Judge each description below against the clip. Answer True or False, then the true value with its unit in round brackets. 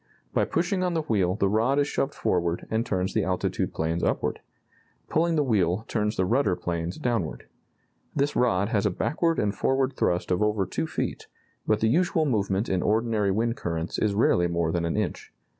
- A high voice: False (105 Hz)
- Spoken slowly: False (190 wpm)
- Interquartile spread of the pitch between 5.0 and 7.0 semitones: True (5.6 semitones)